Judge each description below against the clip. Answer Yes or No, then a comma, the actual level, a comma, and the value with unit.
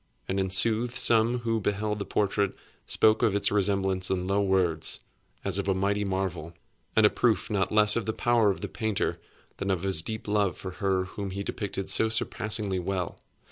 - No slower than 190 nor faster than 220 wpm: Yes, average, 195 wpm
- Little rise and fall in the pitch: Yes, narrow, 2.3 semitones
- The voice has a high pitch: No, low, 100 Hz